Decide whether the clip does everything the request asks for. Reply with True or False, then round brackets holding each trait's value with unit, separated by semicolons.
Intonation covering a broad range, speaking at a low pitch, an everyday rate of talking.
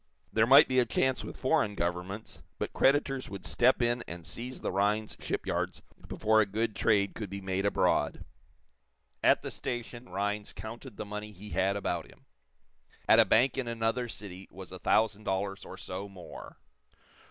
False (3.5 semitones; 105 Hz; 175 wpm)